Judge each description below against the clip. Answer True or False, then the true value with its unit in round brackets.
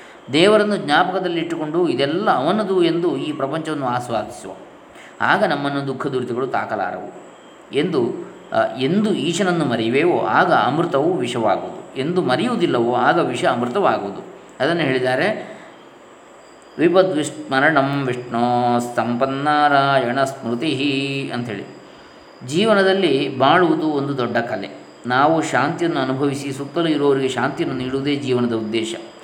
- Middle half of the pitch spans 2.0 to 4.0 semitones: False (4.7 semitones)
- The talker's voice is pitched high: False (140 Hz)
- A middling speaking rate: True (95 wpm)